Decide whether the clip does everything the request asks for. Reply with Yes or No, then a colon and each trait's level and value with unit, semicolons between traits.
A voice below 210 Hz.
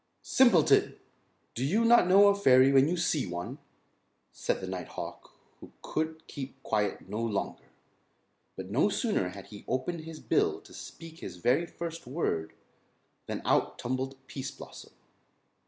Yes: low, 135 Hz